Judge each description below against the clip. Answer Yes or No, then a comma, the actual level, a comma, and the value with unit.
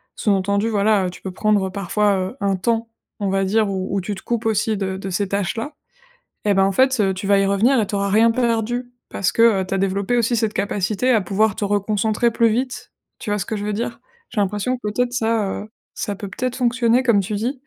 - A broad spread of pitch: No, average, 2.8 semitones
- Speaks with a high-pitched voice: Yes, high, 210 Hz